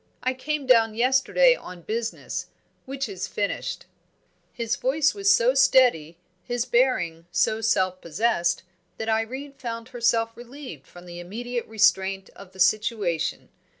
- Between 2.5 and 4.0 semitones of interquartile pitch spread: No, average, 5.3 semitones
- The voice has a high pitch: Yes, high, 230 Hz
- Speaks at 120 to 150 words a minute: Yes, slow, 135 wpm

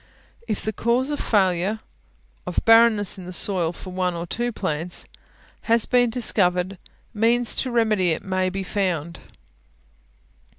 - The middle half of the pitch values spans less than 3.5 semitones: No, average, 4.1 semitones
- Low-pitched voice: No, high, 195 Hz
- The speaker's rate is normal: Yes, average, 145 wpm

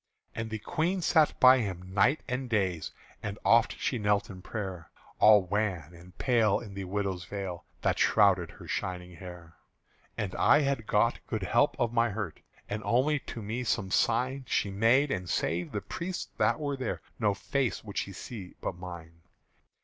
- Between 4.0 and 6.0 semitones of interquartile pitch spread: Yes, average, 4.8 semitones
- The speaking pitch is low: Yes, low, 105 Hz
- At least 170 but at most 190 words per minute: Yes, average, 180 wpm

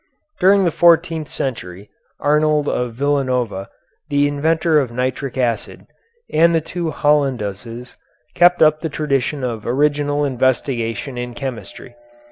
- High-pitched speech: No, medium, 140 Hz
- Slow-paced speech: Yes, slow, 120 wpm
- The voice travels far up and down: No, average, 3.9 semitones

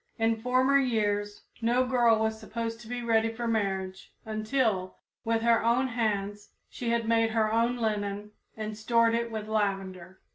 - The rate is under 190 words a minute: Yes, average, 160 wpm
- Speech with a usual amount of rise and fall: No, narrow, 1.9 semitones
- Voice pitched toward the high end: Yes, high, 225 Hz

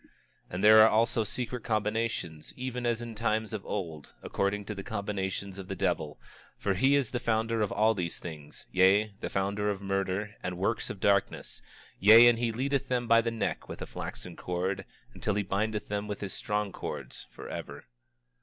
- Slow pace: No, average, 190 wpm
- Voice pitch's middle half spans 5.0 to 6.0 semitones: No, average, 2.8 semitones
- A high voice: No, low, 105 Hz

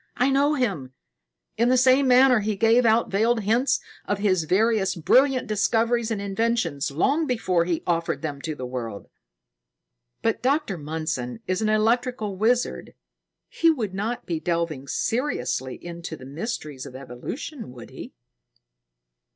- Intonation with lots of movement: Yes, wide, 7.2 semitones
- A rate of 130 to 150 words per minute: Yes, average, 145 wpm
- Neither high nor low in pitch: No, high, 210 Hz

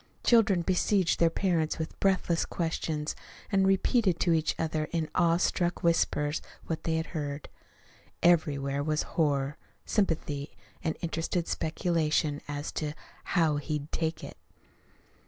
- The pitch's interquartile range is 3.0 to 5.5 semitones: No, narrow, 2.4 semitones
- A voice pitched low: No, medium, 160 Hz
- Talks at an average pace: No, slow, 130 wpm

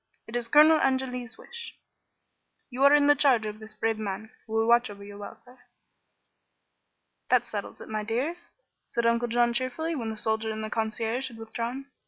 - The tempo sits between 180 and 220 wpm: Yes, average, 185 wpm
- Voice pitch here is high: Yes, high, 235 Hz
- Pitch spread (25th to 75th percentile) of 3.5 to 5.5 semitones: No, average, 3.0 semitones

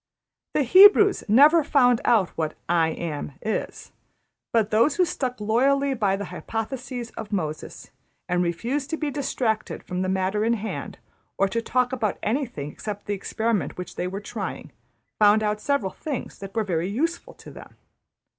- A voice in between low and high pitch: No, high, 220 Hz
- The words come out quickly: No, average, 170 wpm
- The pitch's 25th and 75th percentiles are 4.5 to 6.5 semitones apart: Yes, average, 5.3 semitones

